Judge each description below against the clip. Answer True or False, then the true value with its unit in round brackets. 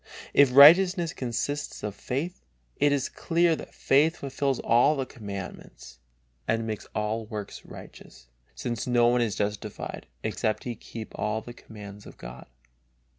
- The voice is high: False (120 Hz)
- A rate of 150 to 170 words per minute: False (140 wpm)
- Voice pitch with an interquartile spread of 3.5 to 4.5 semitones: False (5.0 semitones)